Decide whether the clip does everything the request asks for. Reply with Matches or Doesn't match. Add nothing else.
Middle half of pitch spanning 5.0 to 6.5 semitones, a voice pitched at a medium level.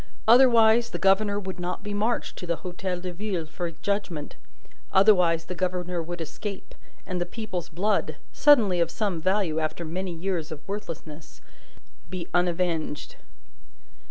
Doesn't match